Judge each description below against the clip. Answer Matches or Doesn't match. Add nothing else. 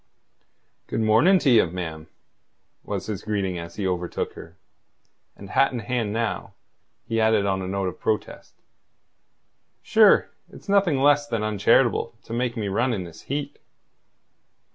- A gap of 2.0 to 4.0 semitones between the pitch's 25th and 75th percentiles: Doesn't match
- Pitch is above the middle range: Doesn't match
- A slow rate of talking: Doesn't match